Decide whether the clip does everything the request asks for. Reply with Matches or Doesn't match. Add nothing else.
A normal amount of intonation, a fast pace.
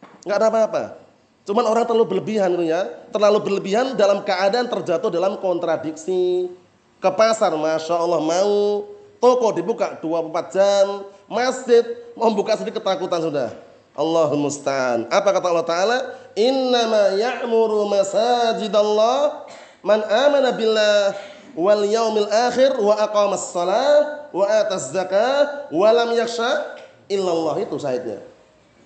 Doesn't match